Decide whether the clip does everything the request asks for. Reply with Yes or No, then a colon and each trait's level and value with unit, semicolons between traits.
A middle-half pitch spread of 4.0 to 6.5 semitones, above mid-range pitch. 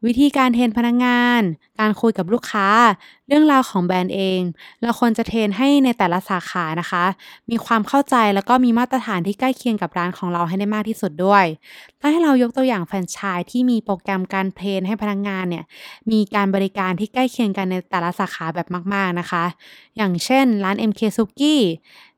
Yes: average, 4.5 semitones; high, 205 Hz